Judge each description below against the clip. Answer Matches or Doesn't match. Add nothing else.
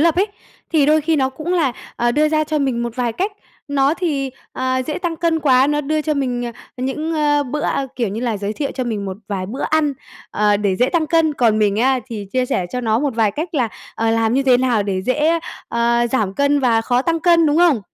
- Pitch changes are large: Doesn't match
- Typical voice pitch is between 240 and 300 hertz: Matches